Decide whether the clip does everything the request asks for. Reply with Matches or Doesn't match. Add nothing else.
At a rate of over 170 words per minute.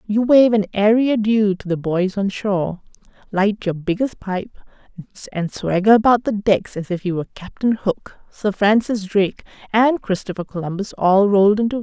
Matches